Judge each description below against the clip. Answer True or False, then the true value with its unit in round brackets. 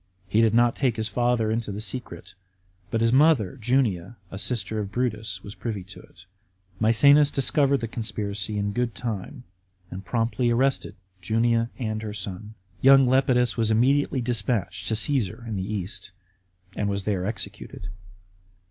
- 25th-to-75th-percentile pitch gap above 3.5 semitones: False (3.1 semitones)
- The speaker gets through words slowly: False (155 wpm)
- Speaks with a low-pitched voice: True (115 Hz)